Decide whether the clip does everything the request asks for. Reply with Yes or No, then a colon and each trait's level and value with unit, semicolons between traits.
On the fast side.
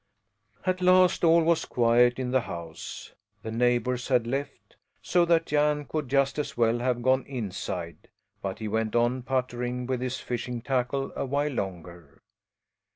No: average, 160 wpm